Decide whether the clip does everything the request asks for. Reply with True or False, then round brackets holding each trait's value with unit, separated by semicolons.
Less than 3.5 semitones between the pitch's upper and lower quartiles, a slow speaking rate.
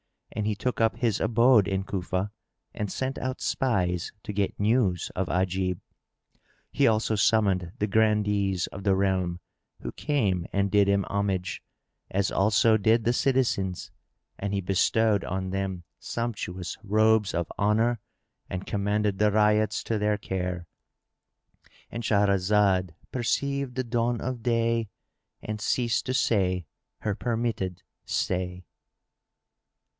True (3.1 semitones; 130 wpm)